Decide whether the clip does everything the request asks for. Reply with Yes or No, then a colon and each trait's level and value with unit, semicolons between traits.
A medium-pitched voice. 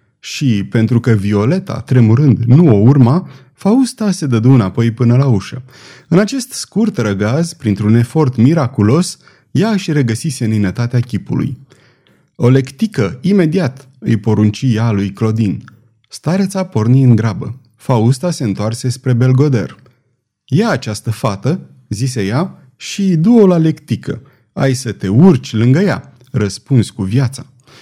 No: low, 130 Hz